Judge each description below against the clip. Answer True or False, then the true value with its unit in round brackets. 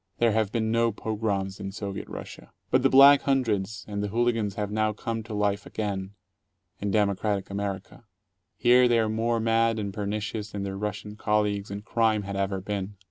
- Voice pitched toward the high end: False (105 Hz)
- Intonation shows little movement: True (2.1 semitones)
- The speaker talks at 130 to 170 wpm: False (190 wpm)